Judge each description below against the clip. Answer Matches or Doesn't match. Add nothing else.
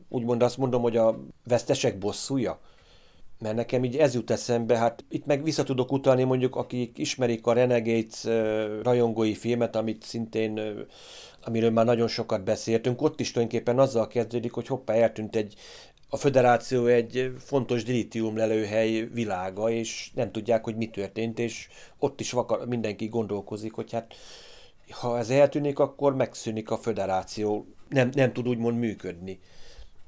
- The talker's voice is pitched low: Matches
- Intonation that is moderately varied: Doesn't match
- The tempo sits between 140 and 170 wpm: Matches